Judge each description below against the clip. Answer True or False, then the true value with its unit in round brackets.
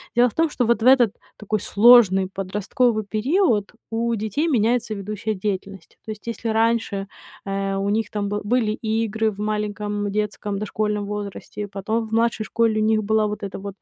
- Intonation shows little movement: True (2.0 semitones)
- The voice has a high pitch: True (215 Hz)